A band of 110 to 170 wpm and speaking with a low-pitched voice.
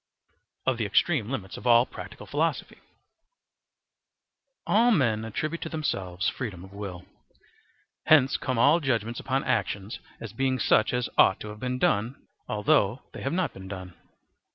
Yes: average, 155 wpm; low, 120 Hz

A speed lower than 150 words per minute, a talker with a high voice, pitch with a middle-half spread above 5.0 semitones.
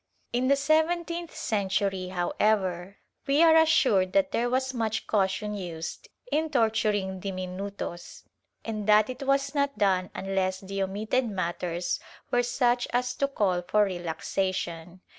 Yes: average, 140 wpm; high, 210 Hz; wide, 5.5 semitones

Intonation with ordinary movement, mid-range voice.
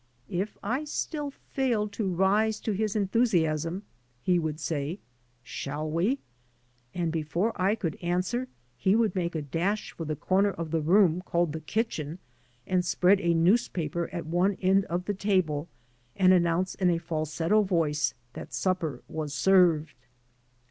Yes: average, 4.0 semitones; medium, 175 Hz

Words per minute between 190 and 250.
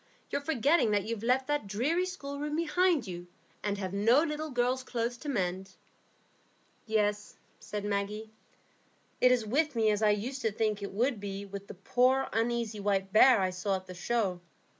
No: average, 180 wpm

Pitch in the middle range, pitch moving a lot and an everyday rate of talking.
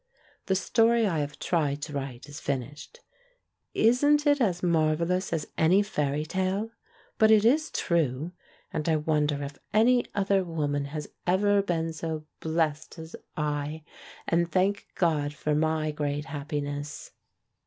No: medium, 160 Hz; average, 4.5 semitones; average, 150 wpm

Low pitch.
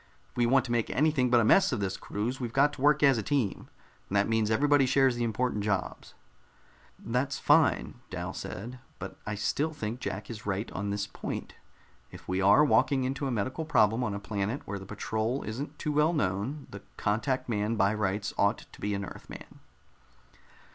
Yes: low, 115 Hz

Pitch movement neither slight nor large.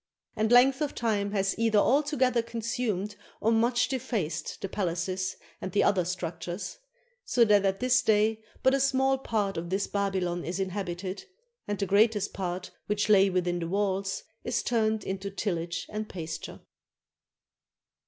Yes: average, 3.6 semitones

